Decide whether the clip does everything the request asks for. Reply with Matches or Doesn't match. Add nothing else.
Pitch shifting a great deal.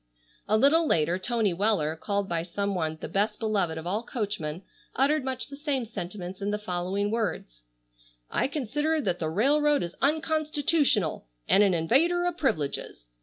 Matches